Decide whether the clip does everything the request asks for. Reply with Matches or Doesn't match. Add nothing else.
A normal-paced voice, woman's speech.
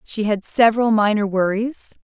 Matches